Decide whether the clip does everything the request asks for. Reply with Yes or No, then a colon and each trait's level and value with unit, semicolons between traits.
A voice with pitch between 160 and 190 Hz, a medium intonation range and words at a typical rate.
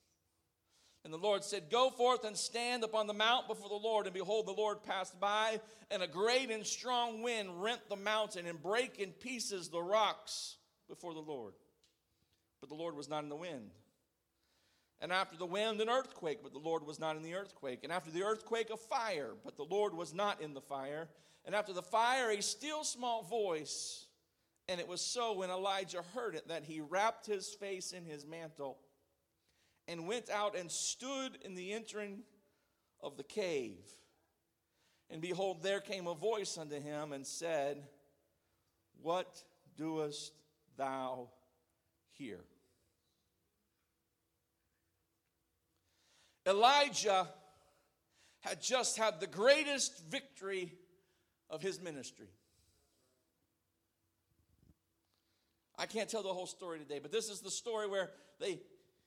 No: medium, 185 Hz; wide, 7.1 semitones; average, 150 wpm